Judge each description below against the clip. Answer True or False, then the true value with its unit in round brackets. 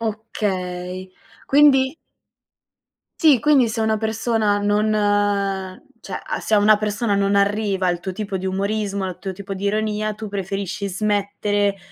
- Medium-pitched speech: False (205 Hz)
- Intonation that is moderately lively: False (1.8 semitones)